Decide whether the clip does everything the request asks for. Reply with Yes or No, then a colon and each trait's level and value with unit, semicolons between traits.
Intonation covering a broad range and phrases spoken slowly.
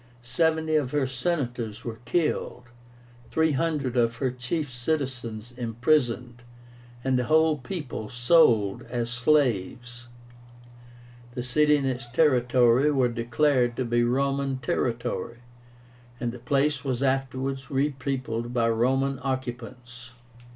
No: narrow, 2.5 semitones; slow, 115 wpm